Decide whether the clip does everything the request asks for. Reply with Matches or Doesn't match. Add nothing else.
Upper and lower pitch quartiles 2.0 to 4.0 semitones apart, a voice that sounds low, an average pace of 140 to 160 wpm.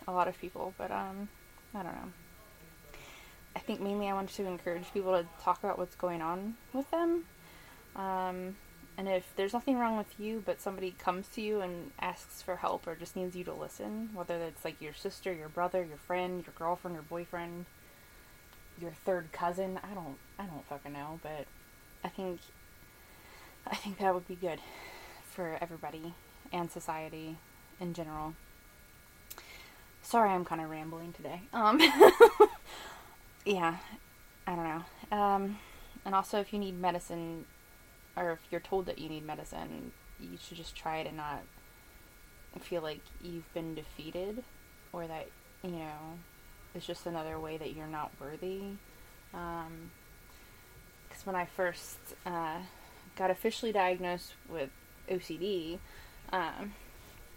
Doesn't match